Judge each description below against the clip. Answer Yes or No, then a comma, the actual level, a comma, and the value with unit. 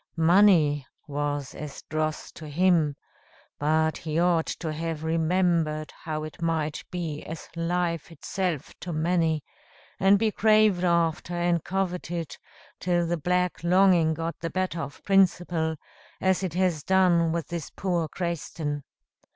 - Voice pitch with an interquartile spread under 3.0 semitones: Yes, narrow, 2.4 semitones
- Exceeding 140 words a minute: No, slow, 135 wpm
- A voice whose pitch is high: No, medium, 170 Hz